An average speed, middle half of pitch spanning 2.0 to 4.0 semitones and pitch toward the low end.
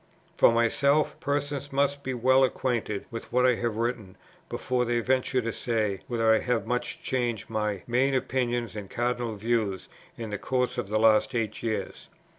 Yes: average, 175 wpm; narrow, 2.5 semitones; low, 120 Hz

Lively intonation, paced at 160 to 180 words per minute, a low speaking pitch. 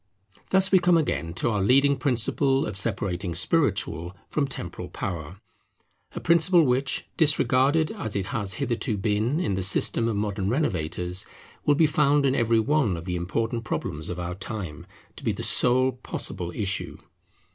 Yes: wide, 7.0 semitones; average, 165 wpm; low, 115 Hz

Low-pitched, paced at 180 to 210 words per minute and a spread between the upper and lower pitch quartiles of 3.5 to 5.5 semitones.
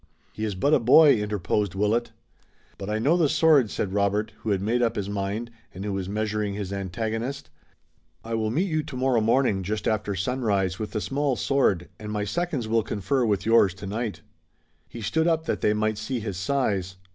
Yes: low, 110 Hz; average, 195 wpm; average, 3.8 semitones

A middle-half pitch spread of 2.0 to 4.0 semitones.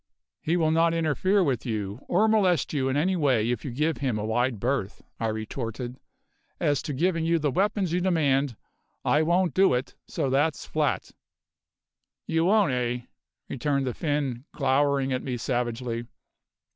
No: average, 5.1 semitones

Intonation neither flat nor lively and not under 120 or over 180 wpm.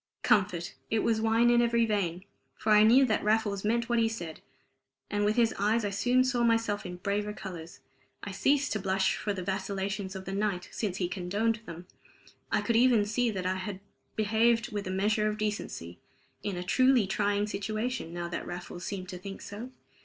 No: average, 3.0 semitones; average, 200 wpm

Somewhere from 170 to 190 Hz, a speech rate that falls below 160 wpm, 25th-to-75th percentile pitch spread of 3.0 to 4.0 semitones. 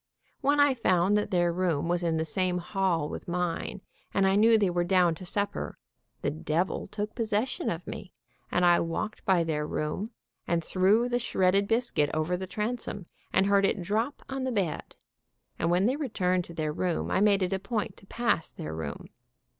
No: medium, 185 Hz; average, 200 wpm; average, 3.6 semitones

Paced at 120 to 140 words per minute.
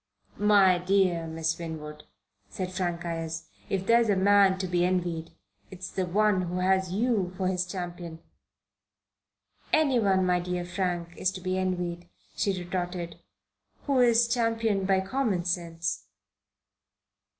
Yes: slow, 135 wpm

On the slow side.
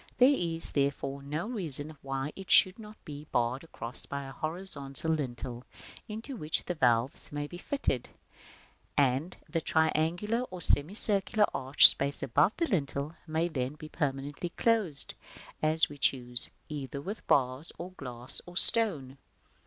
No: average, 145 wpm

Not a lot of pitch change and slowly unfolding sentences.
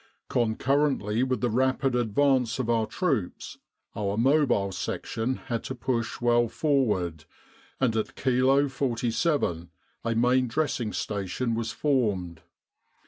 No: average, 3.2 semitones; slow, 120 wpm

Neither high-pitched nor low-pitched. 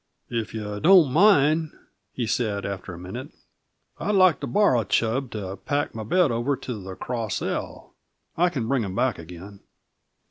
No: low, 120 Hz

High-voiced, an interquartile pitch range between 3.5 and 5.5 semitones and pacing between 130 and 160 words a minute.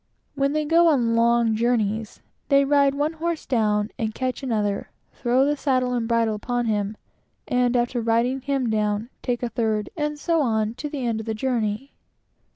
No: high, 240 Hz; average, 3.9 semitones; average, 180 wpm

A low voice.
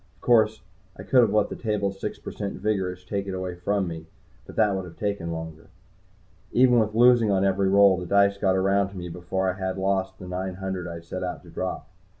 Yes: very low, 95 Hz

